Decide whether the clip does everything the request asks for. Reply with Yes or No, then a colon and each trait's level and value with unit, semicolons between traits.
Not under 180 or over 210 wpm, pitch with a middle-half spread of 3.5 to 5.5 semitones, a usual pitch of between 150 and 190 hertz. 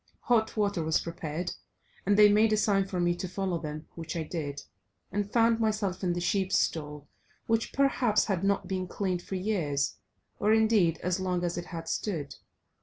Yes: average, 185 wpm; average, 3.8 semitones; medium, 185 Hz